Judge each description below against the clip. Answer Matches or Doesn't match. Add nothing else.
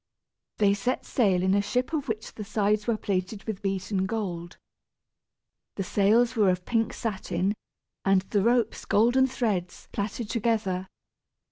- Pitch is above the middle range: Matches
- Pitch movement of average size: Matches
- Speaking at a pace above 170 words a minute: Doesn't match